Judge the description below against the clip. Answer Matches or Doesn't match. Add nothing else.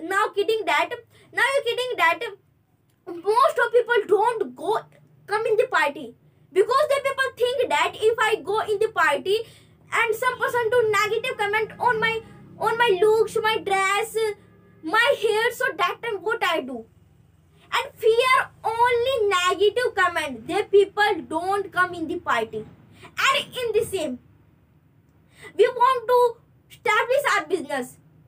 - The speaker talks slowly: Doesn't match